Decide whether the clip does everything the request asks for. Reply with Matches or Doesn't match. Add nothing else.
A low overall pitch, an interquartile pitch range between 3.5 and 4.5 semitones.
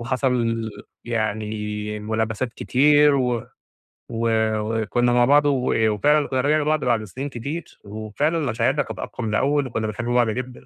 Matches